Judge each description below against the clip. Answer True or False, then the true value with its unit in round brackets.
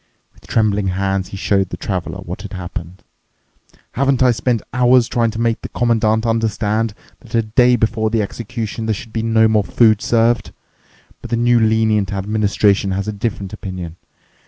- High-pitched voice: False (110 Hz)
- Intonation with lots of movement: False (2.7 semitones)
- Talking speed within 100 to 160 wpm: False (175 wpm)